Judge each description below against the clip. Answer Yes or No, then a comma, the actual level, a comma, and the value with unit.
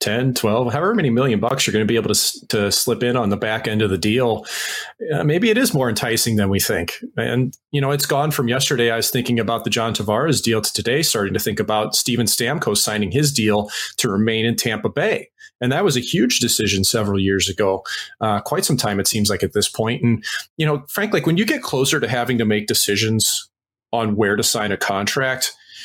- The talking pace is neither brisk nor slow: No, fast, 230 wpm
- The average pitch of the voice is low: Yes, low, 115 Hz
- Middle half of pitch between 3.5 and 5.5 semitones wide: Yes, average, 4.0 semitones